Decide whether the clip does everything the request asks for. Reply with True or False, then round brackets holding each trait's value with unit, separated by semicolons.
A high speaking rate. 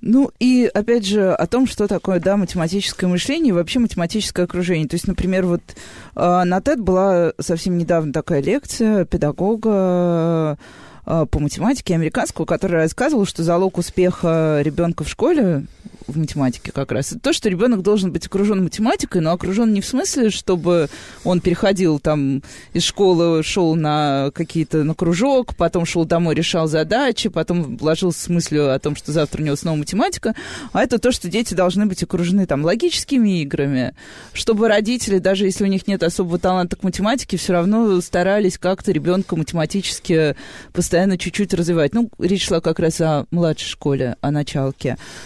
True (165 wpm)